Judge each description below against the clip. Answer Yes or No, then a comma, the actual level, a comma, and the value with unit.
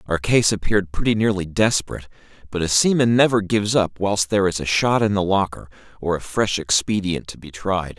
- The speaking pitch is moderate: No, low, 100 Hz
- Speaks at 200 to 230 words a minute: Yes, fast, 205 wpm